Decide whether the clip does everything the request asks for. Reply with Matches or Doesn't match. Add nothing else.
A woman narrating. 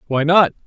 Doesn't match